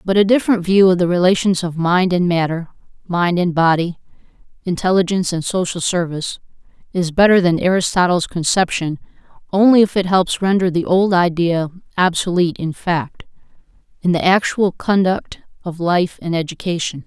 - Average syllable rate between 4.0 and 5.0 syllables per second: No, 5.3 syllables/s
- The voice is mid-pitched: Yes, medium, 180 Hz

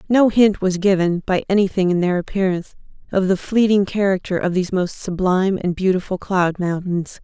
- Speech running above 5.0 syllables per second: Yes, 5.4 syllables/s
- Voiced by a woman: Yes, female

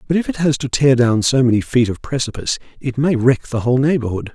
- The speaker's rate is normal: No, fast, 250 wpm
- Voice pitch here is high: No, low, 130 Hz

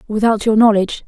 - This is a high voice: Yes, high, 215 Hz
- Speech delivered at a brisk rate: No, average, 170 wpm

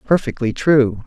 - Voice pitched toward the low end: Yes, low, 130 Hz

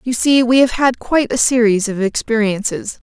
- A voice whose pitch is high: Yes, high, 235 Hz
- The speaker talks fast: No, average, 195 wpm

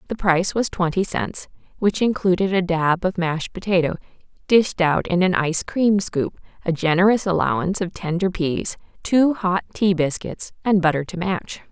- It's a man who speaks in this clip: No, female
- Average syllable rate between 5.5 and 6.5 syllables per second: No, 4.8 syllables/s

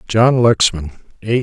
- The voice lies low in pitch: Yes, low, 110 Hz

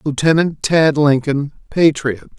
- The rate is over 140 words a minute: No, slow, 100 wpm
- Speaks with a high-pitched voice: No, medium, 145 Hz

